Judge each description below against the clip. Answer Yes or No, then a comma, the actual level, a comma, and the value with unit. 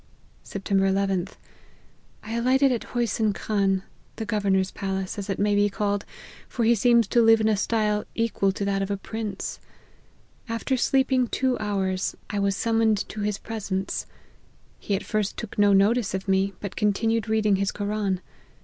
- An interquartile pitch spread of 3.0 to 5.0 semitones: No, narrow, 2.4 semitones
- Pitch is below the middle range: No, high, 205 Hz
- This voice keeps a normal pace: Yes, average, 170 wpm